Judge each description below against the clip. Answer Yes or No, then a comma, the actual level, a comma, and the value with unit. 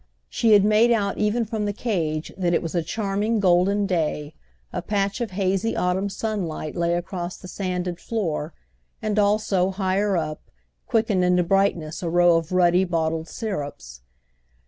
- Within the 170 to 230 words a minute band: No, average, 160 wpm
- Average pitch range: Yes, average, 3.3 semitones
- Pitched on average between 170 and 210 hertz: Yes, medium, 185 Hz